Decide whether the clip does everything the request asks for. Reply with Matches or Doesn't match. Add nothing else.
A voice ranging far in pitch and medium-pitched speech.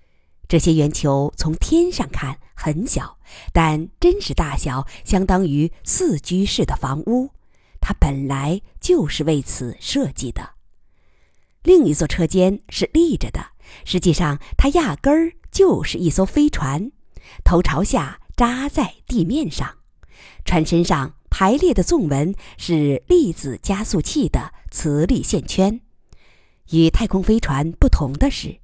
Matches